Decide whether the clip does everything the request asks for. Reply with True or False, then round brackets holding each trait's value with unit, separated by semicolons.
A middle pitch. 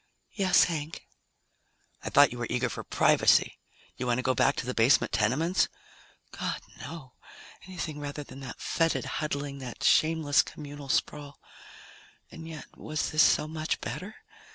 True (145 Hz)